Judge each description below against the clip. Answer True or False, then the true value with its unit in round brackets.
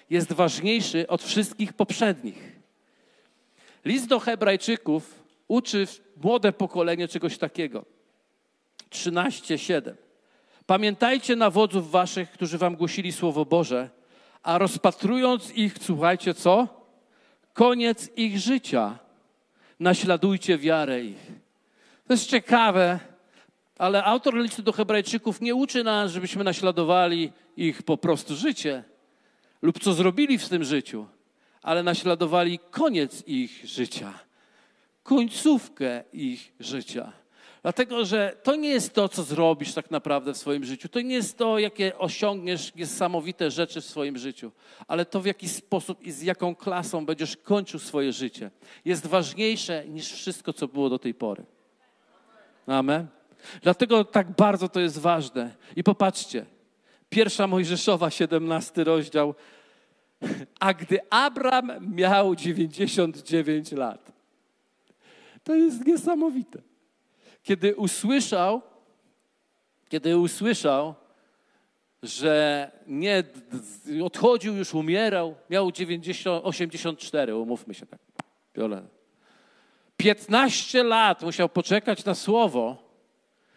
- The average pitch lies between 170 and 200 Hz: True (185 Hz)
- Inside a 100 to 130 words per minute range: True (110 wpm)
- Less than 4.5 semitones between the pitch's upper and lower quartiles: False (5.0 semitones)